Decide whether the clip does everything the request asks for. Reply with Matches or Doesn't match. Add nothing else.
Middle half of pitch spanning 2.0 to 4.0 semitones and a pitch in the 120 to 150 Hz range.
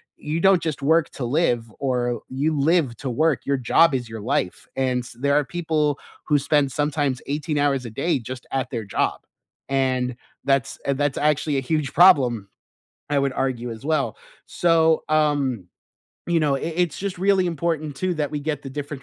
Matches